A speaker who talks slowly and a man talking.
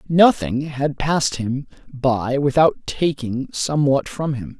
Yes: slow, 130 wpm; male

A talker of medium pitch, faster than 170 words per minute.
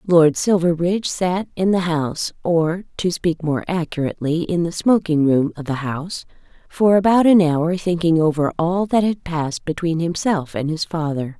No: medium, 170 Hz; average, 165 wpm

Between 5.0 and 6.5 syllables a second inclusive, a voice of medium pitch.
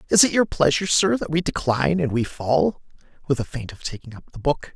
Yes: 6.0 syllables/s; medium, 145 Hz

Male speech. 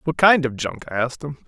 Yes: male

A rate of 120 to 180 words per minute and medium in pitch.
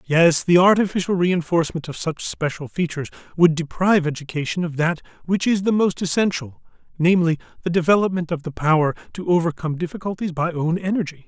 Yes: average, 160 wpm; medium, 170 Hz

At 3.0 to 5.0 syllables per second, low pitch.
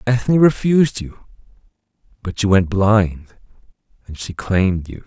Yes: 4.5 syllables/s; low, 105 Hz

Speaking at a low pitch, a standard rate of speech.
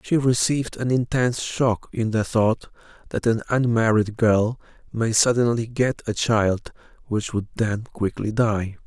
Yes: low, 115 Hz; average, 150 wpm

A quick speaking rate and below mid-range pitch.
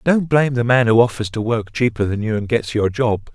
Yes: fast, 270 wpm; low, 115 Hz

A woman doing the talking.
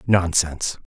No: male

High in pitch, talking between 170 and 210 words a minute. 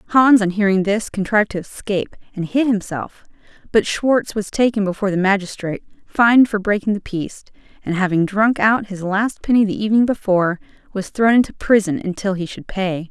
Yes: high, 205 Hz; average, 185 wpm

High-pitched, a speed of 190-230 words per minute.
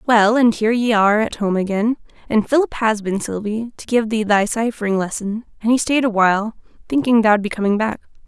Yes: high, 220 Hz; fast, 205 wpm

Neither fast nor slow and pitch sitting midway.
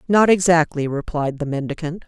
Yes: average, 145 wpm; medium, 160 Hz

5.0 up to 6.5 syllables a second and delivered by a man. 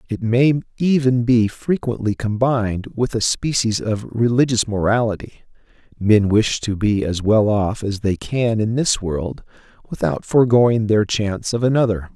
No: 4.8 syllables/s; male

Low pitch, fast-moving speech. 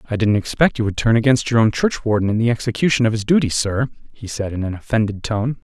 Yes: low, 115 Hz; fast, 240 wpm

